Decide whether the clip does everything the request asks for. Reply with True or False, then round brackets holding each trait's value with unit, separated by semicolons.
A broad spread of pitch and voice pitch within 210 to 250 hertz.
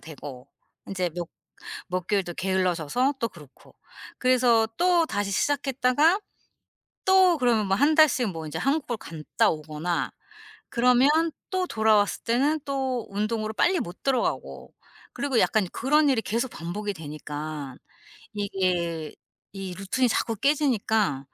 True (7.1 semitones; 215 Hz)